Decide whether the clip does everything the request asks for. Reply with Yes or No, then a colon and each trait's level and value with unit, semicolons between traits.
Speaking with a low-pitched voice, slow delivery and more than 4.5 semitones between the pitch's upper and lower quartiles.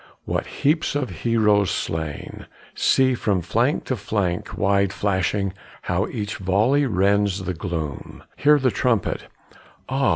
Yes: low, 100 Hz; slow, 130 wpm; average, 5.2 semitones